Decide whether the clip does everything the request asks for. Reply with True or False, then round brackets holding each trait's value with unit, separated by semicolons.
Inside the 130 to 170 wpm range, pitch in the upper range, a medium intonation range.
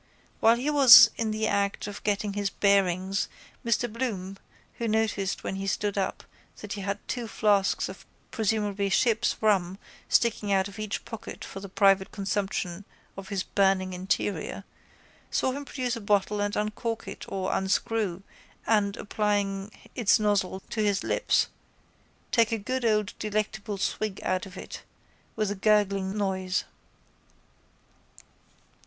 False (150 wpm; 205 Hz; 2.0 semitones)